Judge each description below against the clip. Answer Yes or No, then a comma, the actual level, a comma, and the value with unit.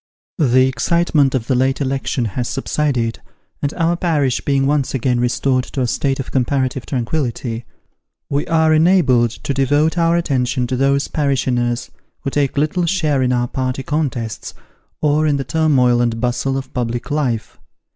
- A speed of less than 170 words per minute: Yes, average, 160 wpm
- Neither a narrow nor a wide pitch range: Yes, average, 3.2 semitones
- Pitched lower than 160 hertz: Yes, low, 135 Hz